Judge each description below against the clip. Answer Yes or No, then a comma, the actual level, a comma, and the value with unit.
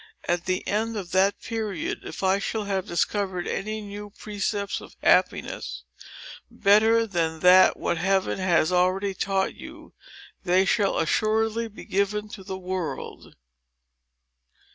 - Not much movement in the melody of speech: Yes, narrow, 2.3 semitones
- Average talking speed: No, slow, 130 wpm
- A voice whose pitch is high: Yes, high, 195 Hz